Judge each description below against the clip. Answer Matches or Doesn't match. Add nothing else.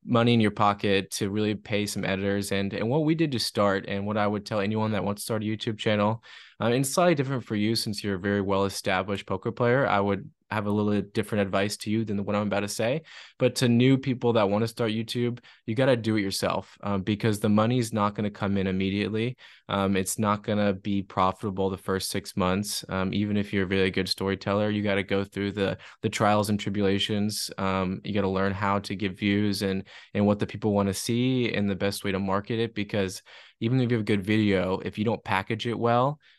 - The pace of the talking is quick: Matches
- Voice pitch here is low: Matches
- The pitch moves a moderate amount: Doesn't match